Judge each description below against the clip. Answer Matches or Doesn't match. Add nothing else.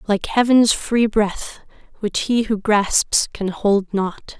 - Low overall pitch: Doesn't match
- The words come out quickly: Doesn't match